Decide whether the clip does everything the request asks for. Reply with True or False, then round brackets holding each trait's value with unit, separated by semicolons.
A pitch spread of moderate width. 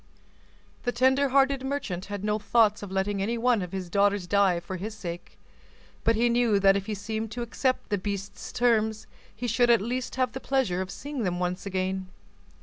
True (3.9 semitones)